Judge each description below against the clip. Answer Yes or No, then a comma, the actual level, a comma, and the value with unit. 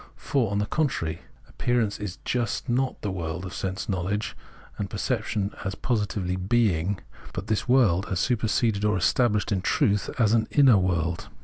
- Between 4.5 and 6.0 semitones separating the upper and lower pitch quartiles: No, average, 4.0 semitones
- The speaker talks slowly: No, average, 165 wpm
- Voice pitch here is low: Yes, low, 105 Hz